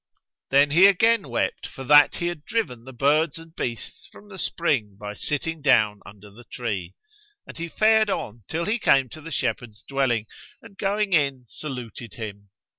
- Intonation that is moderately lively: No, wide, 6.5 semitones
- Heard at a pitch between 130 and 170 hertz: Yes, medium, 140 Hz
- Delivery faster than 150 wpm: Yes, average, 180 wpm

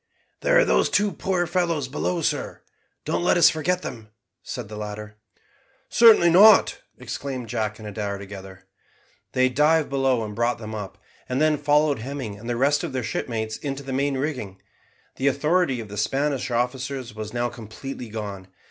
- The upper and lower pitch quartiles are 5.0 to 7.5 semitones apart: Yes, wide, 5.4 semitones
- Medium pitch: No, low, 130 Hz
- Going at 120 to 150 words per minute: No, average, 175 wpm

